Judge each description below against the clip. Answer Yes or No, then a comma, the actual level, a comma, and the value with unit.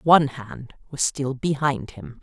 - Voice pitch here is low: Yes, low, 130 Hz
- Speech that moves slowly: No, average, 160 wpm